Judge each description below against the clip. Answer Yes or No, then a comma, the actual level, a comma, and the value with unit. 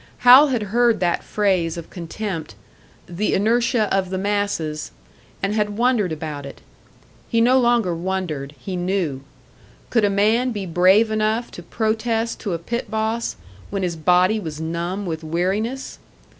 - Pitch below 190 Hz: No, high, 200 Hz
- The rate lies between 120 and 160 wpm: Yes, average, 155 wpm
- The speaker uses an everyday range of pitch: Yes, average, 4.6 semitones